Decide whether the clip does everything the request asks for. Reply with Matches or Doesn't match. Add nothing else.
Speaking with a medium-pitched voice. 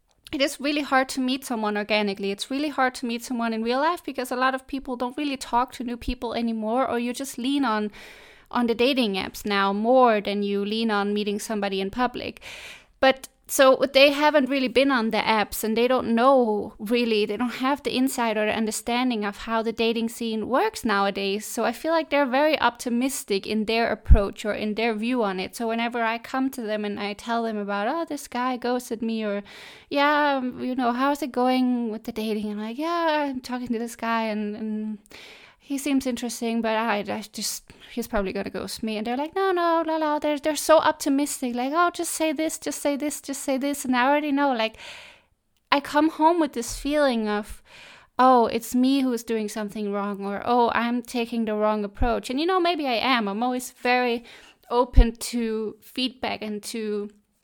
Doesn't match